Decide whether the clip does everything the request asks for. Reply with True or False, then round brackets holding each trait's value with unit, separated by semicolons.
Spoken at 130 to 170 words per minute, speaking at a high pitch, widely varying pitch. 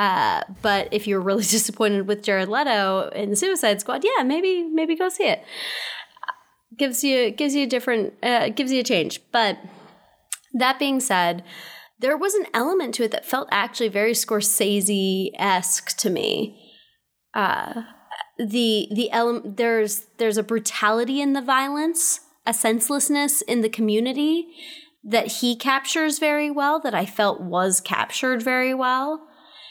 True (150 wpm; 245 Hz; 5.8 semitones)